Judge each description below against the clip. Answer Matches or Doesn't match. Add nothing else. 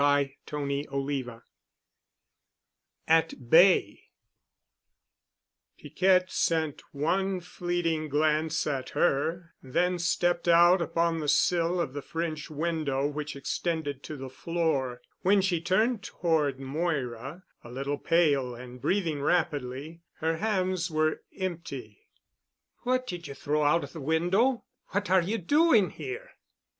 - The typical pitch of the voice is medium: Matches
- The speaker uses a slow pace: Matches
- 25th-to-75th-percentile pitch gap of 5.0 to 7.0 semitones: Doesn't match